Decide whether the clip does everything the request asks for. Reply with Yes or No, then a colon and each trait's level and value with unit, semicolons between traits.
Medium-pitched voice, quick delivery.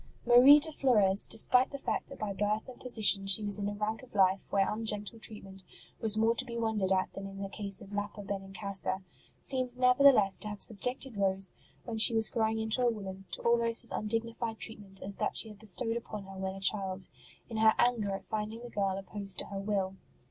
No: high, 210 Hz; fast, 220 wpm